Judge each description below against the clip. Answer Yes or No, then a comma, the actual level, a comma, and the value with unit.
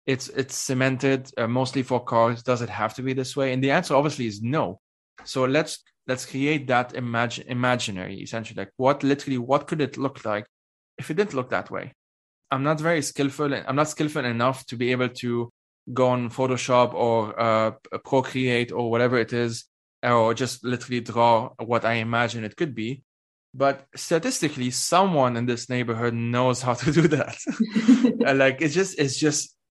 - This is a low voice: Yes, low, 130 Hz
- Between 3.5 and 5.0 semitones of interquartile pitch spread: No, average, 2.7 semitones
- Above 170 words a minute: Yes, average, 180 wpm